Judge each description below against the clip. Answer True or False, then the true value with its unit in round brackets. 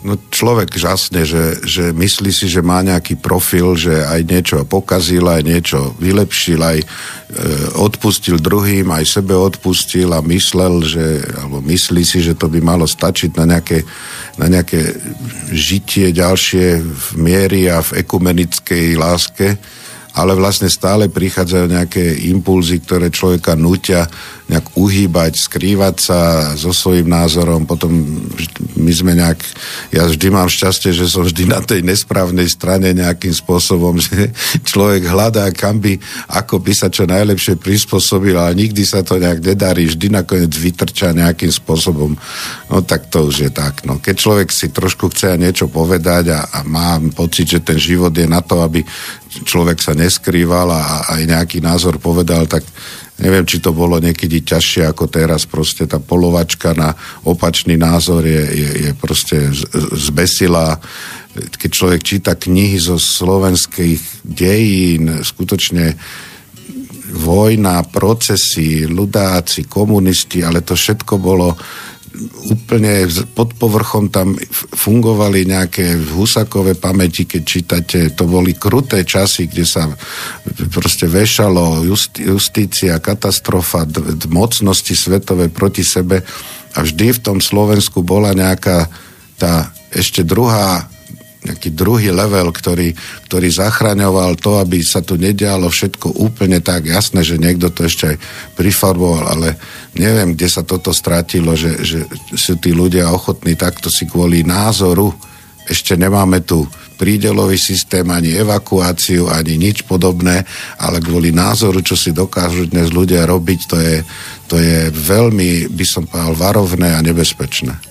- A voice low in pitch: True (90 Hz)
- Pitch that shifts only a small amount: True (2.3 semitones)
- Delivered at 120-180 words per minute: True (140 wpm)